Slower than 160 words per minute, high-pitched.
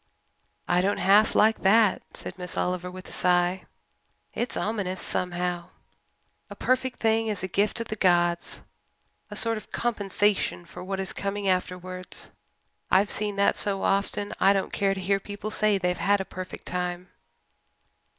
No: average, 165 wpm; high, 195 Hz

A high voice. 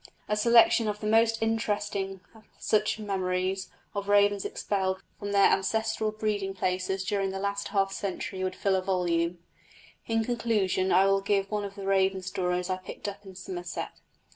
Yes: high, 195 Hz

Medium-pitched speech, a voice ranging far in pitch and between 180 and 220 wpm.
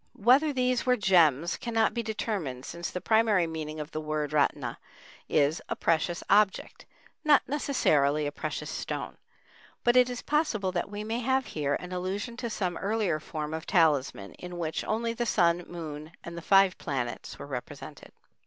No: medium, 180 Hz; wide, 6.6 semitones; average, 170 wpm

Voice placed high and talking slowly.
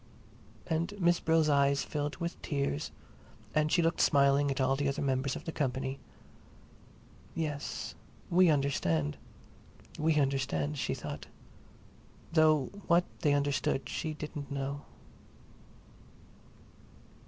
No: medium, 145 Hz; slow, 110 wpm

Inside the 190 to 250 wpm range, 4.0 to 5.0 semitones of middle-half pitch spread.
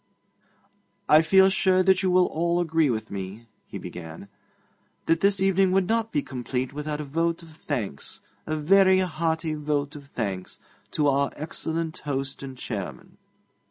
No: average, 155 wpm; average, 4.7 semitones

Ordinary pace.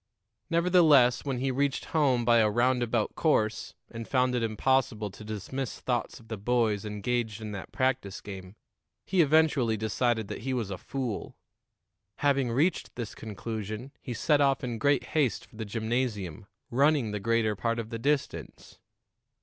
Yes: average, 160 wpm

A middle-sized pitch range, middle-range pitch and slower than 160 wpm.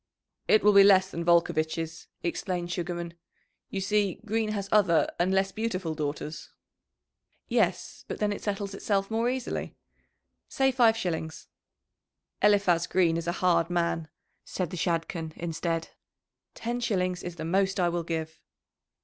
Yes: average, 3.2 semitones; medium, 180 Hz; average, 145 wpm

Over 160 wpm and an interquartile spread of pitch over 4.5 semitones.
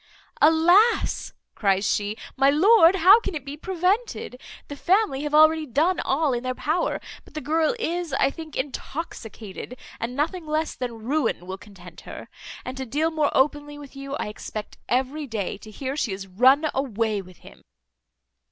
Yes: average, 170 wpm; wide, 5.6 semitones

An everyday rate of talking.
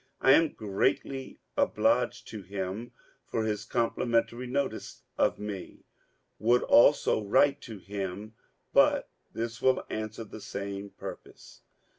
No: slow, 120 wpm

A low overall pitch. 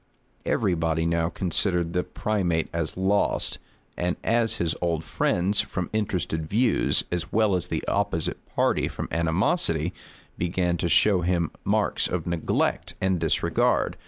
Yes: very low, 90 Hz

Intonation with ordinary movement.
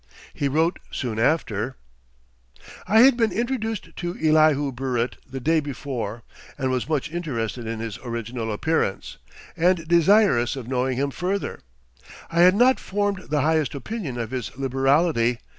No: wide, 6.1 semitones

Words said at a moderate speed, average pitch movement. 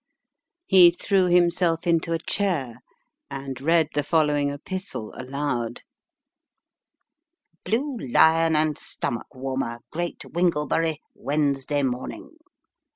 No: slow, 95 wpm; average, 4.0 semitones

